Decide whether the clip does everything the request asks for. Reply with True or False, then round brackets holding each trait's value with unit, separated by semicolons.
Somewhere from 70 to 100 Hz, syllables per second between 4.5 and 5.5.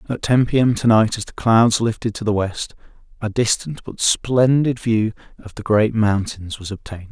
False (110 Hz; 4.9 syllables/s)